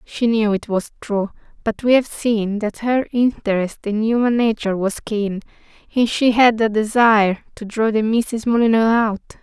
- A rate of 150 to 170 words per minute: No, average, 180 wpm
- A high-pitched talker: Yes, high, 220 Hz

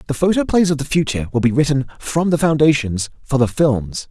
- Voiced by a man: Yes, male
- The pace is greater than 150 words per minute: Yes, fast, 205 wpm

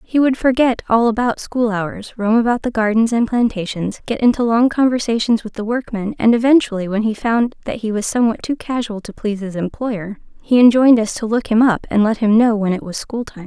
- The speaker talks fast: Yes, fast, 225 wpm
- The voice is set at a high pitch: Yes, high, 225 Hz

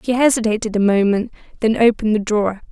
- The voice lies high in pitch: Yes, high, 220 Hz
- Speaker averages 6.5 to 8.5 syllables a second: Yes, 6.7 syllables/s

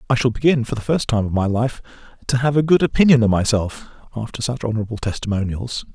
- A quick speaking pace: Yes, fast, 210 wpm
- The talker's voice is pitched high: No, low, 120 Hz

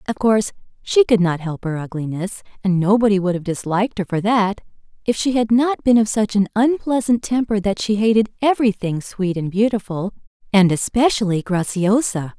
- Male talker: No, female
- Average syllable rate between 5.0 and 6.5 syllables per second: Yes, 5.3 syllables/s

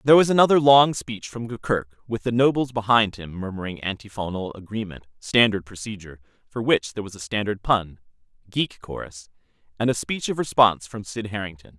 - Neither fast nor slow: Yes, average, 165 wpm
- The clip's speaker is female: No, male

